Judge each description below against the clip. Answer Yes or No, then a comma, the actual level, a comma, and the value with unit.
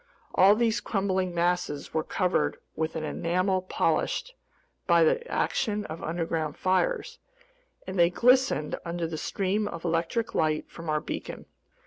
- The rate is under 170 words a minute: Yes, average, 140 wpm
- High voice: No, medium, 180 Hz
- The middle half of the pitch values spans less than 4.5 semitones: Yes, average, 4.0 semitones